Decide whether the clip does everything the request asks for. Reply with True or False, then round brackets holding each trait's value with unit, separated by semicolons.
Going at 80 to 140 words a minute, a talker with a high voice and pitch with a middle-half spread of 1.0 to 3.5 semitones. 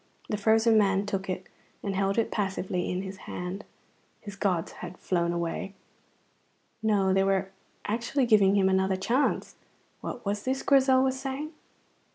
False (155 wpm; 200 Hz; 3.0 semitones)